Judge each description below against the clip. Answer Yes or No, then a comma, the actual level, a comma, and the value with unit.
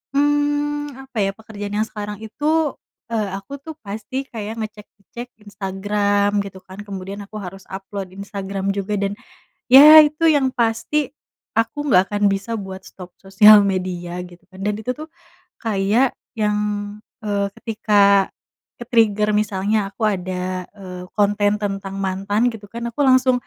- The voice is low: No, high, 205 Hz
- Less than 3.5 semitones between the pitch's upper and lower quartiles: Yes, average, 3.1 semitones